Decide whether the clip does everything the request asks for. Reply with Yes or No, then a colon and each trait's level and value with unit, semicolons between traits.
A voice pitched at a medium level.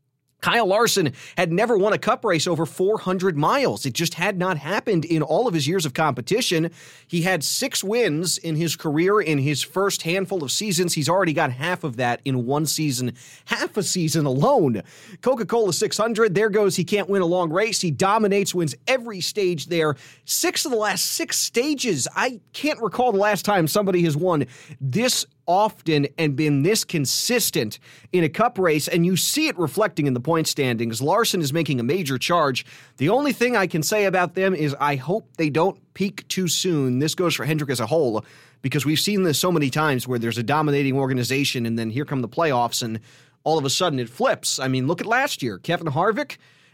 Yes: medium, 165 Hz